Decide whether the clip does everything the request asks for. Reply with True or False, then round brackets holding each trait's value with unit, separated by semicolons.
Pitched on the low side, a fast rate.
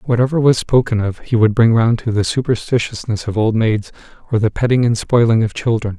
True (115 Hz; 210 wpm)